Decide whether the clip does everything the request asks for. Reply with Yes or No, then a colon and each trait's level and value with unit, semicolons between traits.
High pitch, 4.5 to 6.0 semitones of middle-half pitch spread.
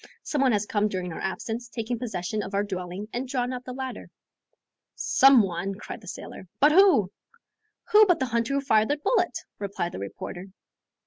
Yes: high, 225 Hz; average, 5.1 semitones